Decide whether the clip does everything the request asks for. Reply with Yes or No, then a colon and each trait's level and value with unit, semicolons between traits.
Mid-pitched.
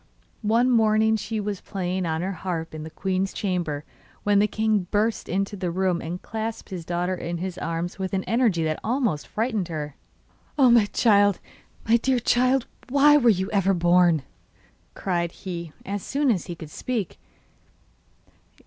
No: high, 195 Hz